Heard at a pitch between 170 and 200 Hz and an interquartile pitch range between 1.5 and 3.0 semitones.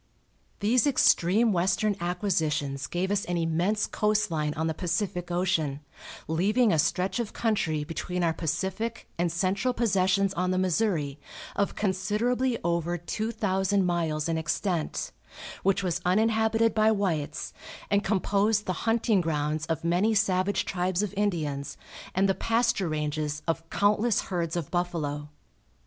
No: medium, 185 Hz; average, 4.1 semitones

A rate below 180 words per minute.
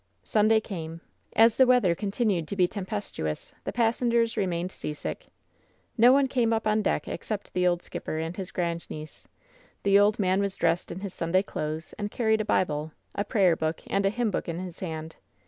No: average, 195 wpm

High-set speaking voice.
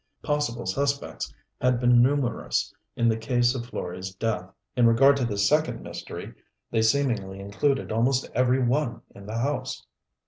No: low, 120 Hz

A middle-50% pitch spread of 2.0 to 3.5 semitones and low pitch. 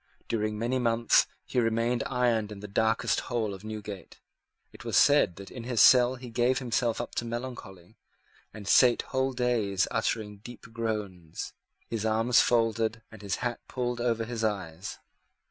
Yes: narrow, 2.5 semitones; low, 115 Hz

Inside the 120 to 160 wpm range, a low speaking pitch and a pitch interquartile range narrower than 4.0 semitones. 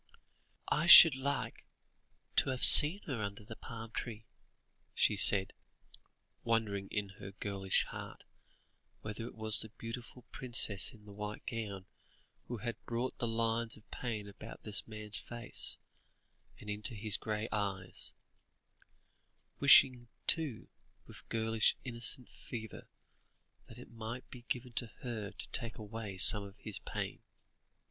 Yes: average, 140 wpm; low, 110 Hz; narrow, 2.4 semitones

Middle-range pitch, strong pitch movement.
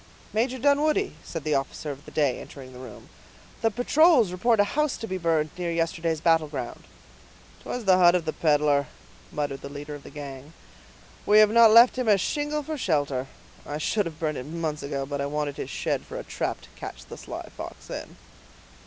Yes: medium, 165 Hz; wide, 7.4 semitones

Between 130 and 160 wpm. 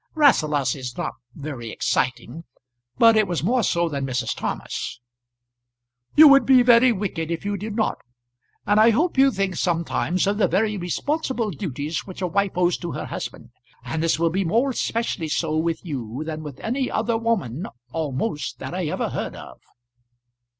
No: average, 175 wpm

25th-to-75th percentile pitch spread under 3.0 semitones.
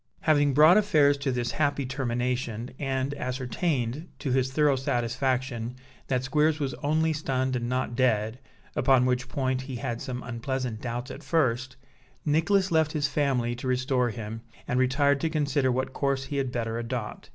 Yes: narrow, 2.6 semitones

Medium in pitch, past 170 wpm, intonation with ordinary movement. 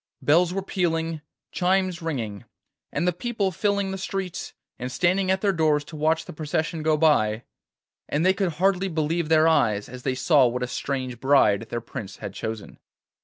No: medium, 160 Hz; average, 180 wpm; wide, 6.1 semitones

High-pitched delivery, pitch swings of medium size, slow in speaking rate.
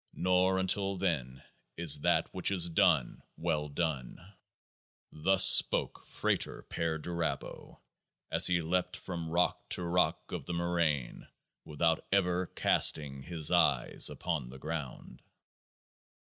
No: very low, 85 Hz; average, 3.0 semitones; slow, 115 wpm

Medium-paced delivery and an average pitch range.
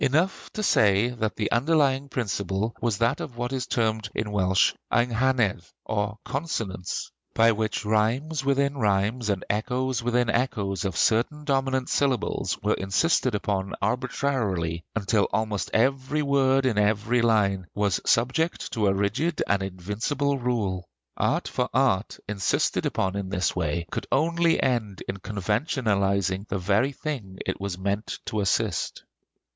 Yes: average, 145 wpm; average, 4.9 semitones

